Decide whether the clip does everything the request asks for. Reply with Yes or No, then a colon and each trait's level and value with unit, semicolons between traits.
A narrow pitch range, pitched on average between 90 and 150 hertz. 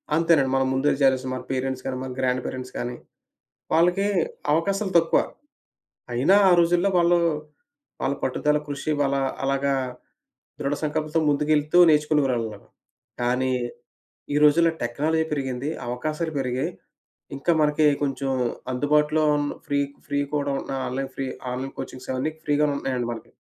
No: average, 3.0 semitones; medium, 140 Hz